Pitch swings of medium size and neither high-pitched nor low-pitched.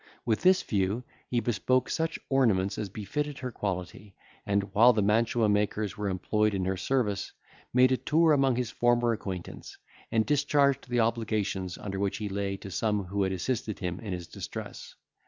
No: average, 4.1 semitones; low, 110 Hz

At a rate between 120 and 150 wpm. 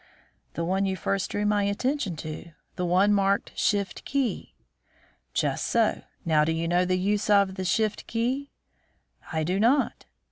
No: average, 165 wpm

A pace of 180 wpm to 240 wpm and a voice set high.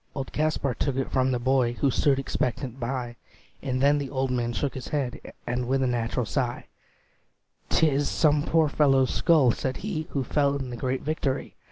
No: average, 195 wpm; low, 135 Hz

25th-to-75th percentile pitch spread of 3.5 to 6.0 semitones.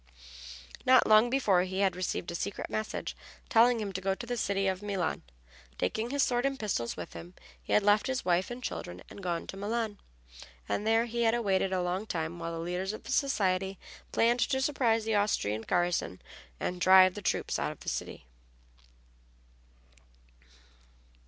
Yes: average, 4.2 semitones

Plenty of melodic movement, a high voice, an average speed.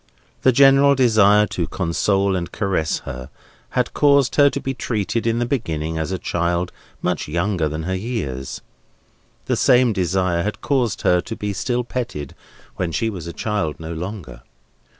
No: wide, 5.7 semitones; very low, 95 Hz; average, 170 wpm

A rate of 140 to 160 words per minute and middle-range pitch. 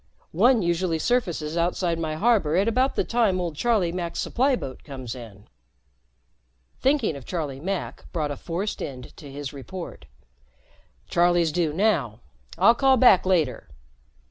Yes: average, 145 wpm; medium, 175 Hz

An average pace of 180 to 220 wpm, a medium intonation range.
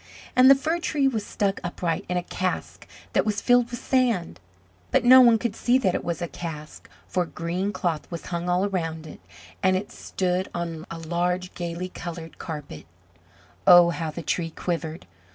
Yes: average, 185 wpm; average, 3.6 semitones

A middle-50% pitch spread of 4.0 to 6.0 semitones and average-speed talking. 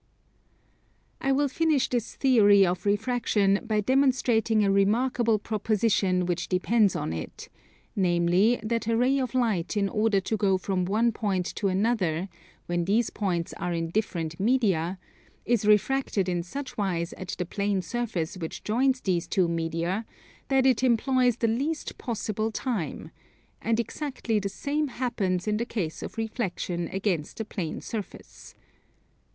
Yes: average, 4.5 semitones; average, 150 wpm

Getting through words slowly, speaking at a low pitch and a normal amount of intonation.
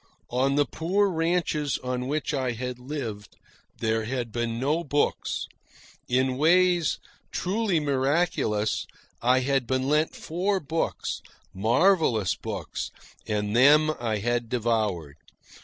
Yes: slow, 120 wpm; low, 130 Hz; average, 5.0 semitones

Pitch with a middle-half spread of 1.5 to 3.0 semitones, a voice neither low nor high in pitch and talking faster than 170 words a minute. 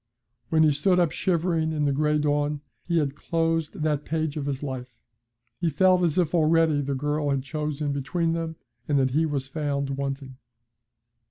Yes: narrow, 2.6 semitones; medium, 150 Hz; average, 180 wpm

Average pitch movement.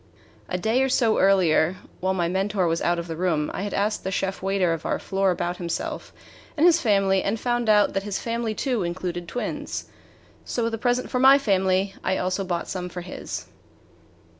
Yes: average, 3.6 semitones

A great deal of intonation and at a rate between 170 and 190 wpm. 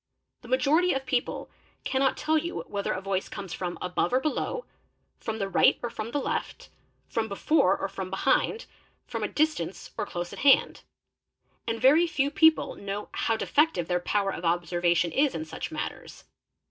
Yes: wide, 7.4 semitones; average, 175 wpm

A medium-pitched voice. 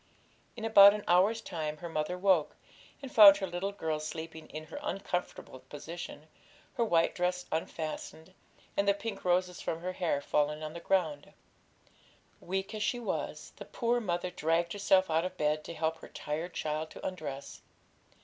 Yes: medium, 175 Hz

